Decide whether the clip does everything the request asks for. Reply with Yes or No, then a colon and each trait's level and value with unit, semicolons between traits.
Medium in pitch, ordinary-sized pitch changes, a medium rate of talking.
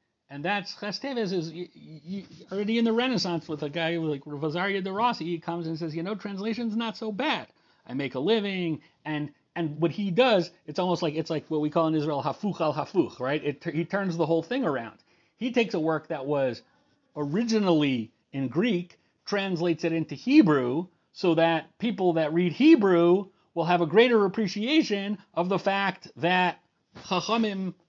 Yes: medium, 175 Hz; average, 4.1 semitones; average, 190 wpm